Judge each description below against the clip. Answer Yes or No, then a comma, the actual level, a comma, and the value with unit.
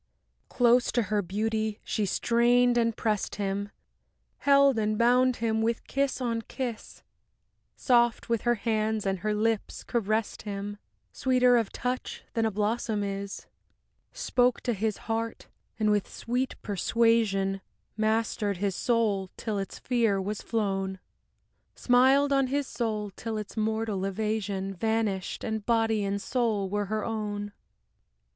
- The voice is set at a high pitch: Yes, high, 220 Hz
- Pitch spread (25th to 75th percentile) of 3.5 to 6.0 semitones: No, narrow, 2.6 semitones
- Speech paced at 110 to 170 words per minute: Yes, average, 140 wpm